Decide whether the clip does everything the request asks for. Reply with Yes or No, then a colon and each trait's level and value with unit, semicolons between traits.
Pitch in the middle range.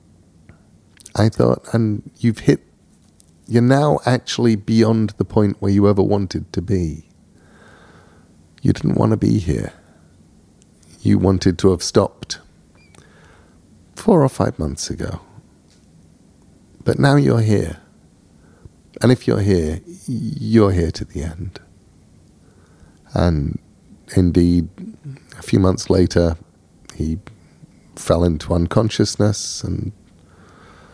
No: very low, 95 Hz